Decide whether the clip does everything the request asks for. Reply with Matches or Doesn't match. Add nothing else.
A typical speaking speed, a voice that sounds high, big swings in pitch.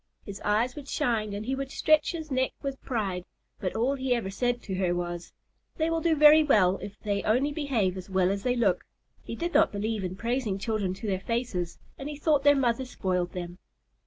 Doesn't match